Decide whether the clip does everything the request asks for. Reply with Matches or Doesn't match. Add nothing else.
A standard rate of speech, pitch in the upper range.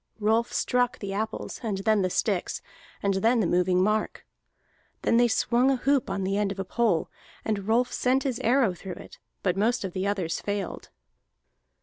Matches